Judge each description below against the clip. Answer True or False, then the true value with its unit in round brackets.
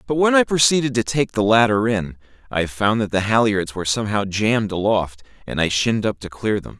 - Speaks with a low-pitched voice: True (110 Hz)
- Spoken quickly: True (220 wpm)